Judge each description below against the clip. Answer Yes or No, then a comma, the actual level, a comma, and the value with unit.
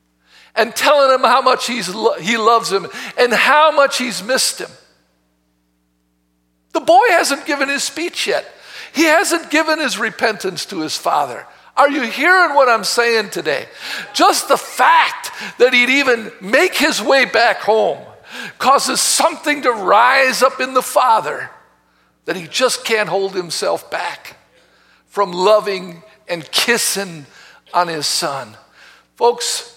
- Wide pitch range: Yes, wide, 6.7 semitones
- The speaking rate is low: No, average, 145 wpm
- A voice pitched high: Yes, high, 235 Hz